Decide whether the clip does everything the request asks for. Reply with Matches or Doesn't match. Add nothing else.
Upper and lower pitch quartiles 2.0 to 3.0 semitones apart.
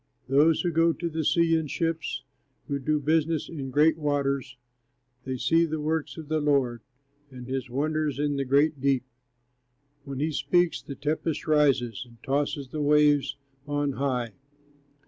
Matches